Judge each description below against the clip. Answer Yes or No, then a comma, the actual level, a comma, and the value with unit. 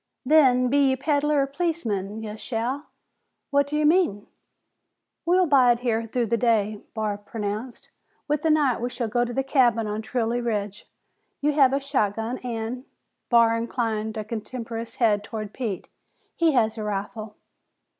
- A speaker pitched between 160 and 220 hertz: No, high, 235 Hz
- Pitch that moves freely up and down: No, average, 3.9 semitones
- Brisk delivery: No, average, 160 wpm